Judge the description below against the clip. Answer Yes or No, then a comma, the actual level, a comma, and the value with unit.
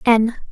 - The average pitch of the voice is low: No, high, 230 Hz